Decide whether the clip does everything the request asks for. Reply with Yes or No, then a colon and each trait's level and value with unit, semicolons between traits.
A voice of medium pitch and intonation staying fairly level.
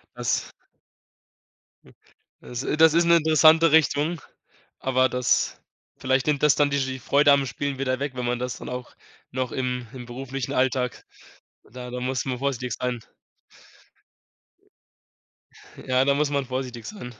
No: low, 130 Hz; narrow, 2.2 semitones